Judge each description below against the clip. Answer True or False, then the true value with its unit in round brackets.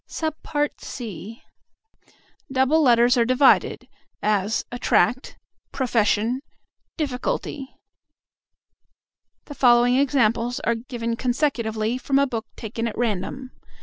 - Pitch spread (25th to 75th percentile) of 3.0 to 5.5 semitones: False (2.6 semitones)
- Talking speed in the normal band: False (105 wpm)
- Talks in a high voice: True (245 Hz)